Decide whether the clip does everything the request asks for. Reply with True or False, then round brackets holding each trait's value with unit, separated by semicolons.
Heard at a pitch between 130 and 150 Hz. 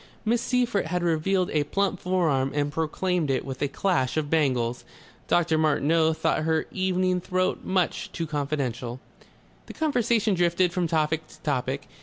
False (160 Hz)